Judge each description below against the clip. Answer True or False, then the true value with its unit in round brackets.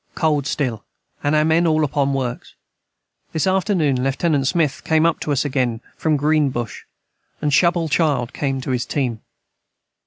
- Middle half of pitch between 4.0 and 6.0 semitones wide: False (3.2 semitones)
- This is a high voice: False (145 Hz)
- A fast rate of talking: False (160 wpm)